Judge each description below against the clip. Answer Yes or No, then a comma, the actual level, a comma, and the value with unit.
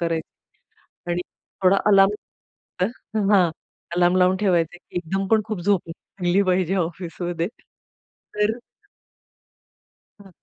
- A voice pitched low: No, medium, 185 Hz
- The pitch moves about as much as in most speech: No, narrow, 2.1 semitones